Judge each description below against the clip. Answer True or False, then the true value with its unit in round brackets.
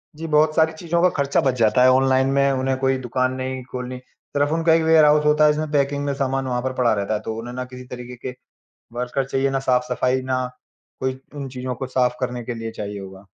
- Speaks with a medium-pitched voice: False (130 Hz)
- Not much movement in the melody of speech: True (2.3 semitones)